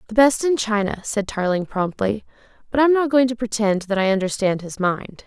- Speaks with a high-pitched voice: Yes, high, 215 Hz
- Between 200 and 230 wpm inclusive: Yes, fast, 205 wpm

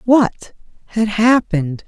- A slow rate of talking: Yes, slow, 95 wpm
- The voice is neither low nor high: No, high, 210 Hz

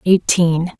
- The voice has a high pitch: No, medium, 175 Hz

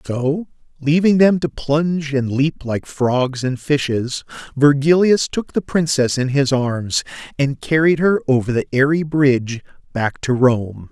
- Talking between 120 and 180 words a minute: Yes, average, 155 wpm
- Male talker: Yes, male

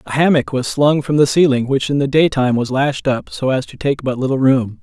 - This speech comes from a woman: No, male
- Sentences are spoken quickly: Yes, fast, 260 wpm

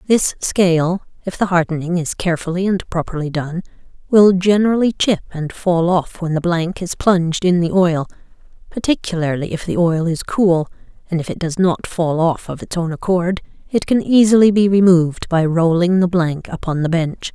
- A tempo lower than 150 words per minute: No, average, 185 wpm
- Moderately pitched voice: Yes, medium, 175 Hz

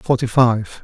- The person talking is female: No, male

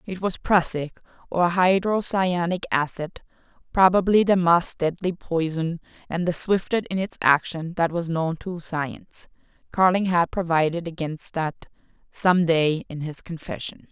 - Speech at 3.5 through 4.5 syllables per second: Yes, 4.3 syllables/s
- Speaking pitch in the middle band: Yes, medium, 170 Hz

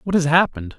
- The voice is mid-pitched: Yes, medium, 155 Hz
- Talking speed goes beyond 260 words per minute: No, fast, 230 wpm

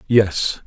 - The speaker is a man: Yes, male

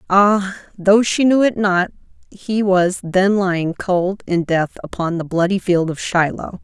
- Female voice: Yes, female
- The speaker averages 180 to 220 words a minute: No, average, 170 wpm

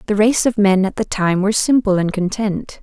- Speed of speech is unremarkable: No, fast, 235 wpm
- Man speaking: No, female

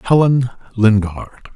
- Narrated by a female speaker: No, male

